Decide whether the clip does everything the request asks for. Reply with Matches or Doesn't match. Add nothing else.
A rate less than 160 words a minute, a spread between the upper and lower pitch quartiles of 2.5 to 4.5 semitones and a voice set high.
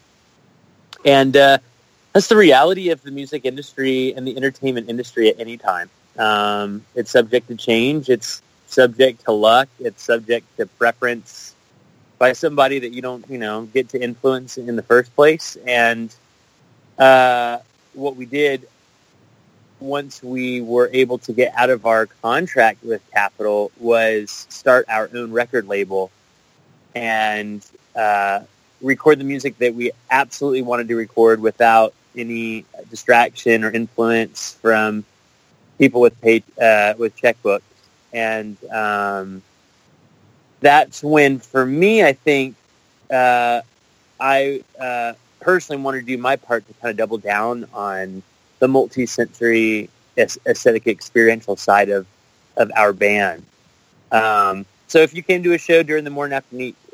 Doesn't match